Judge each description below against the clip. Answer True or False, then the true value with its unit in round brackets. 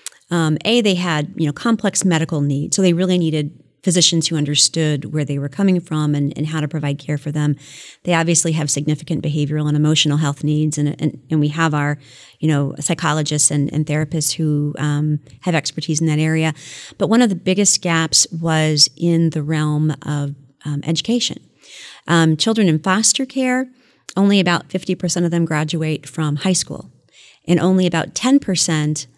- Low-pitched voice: False (155 Hz)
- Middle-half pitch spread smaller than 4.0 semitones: True (2.7 semitones)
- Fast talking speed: False (185 wpm)